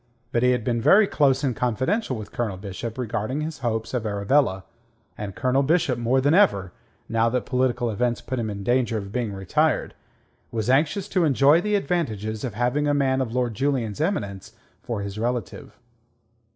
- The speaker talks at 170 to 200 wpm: Yes, average, 180 wpm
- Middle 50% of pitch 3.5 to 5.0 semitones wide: Yes, average, 4.1 semitones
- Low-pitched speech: Yes, low, 125 Hz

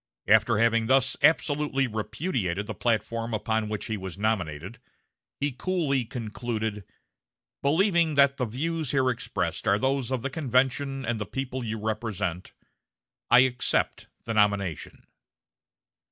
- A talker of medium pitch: No, low, 120 Hz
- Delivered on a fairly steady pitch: No, average, 4.1 semitones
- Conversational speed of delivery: No, slow, 130 wpm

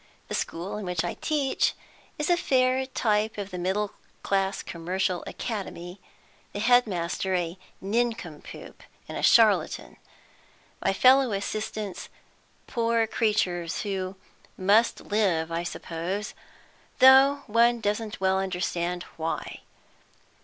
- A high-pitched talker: Yes, high, 200 Hz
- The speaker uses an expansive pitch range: No, average, 4.4 semitones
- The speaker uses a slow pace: Yes, slow, 110 wpm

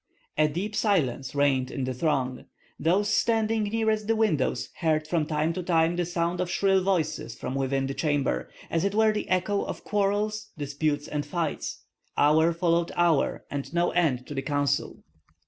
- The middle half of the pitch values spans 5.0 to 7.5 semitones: Yes, average, 5.3 semitones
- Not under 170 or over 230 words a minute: Yes, average, 175 wpm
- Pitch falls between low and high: Yes, medium, 165 Hz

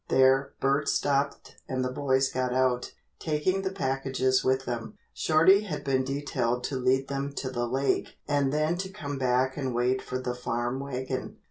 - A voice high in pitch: No, low, 135 Hz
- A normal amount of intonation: No, narrow, 1.8 semitones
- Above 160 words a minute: Yes, average, 175 wpm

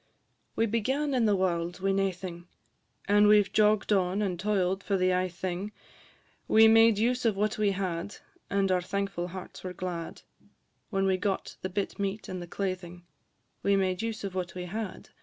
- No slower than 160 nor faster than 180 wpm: No, average, 190 wpm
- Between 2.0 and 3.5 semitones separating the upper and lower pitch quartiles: Yes, narrow, 2.4 semitones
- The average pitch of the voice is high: Yes, high, 195 Hz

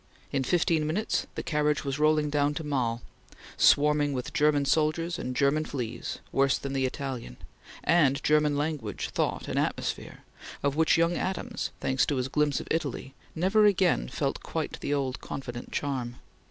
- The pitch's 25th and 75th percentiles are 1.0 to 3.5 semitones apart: Yes, narrow, 2.6 semitones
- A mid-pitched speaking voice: Yes, medium, 145 Hz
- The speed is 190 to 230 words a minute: No, average, 165 wpm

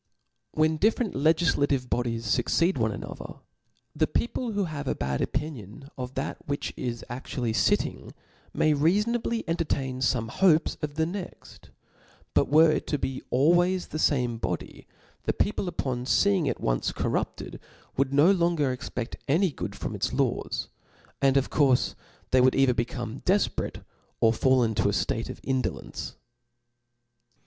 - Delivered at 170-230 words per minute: No, average, 150 wpm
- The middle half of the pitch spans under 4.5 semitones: No, average, 4.9 semitones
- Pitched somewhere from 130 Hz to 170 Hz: Yes, medium, 140 Hz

